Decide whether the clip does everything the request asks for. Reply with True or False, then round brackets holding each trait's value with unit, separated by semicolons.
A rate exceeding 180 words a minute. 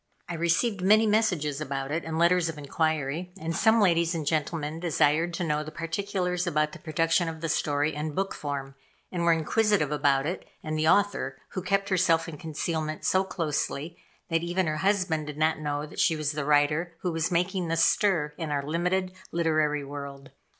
True (190 wpm)